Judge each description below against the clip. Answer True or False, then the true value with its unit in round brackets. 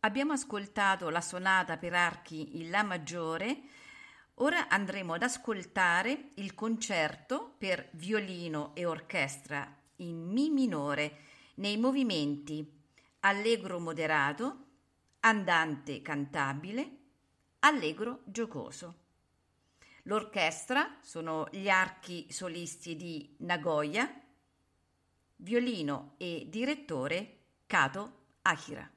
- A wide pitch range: True (6.5 semitones)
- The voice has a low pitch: False (175 Hz)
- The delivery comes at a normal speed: False (85 wpm)